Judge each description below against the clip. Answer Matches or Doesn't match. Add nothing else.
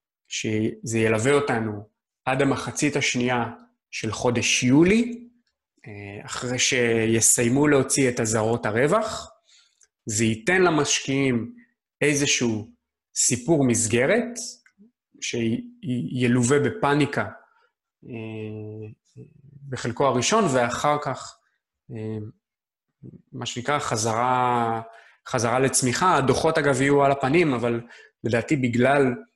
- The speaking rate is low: Matches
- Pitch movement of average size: Matches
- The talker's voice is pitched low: Matches